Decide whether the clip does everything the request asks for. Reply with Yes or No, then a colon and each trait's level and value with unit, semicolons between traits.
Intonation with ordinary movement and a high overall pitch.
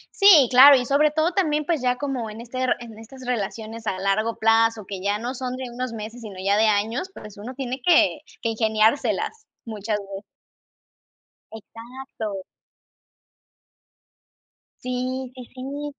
Yes: average, 3.5 semitones; high, 240 Hz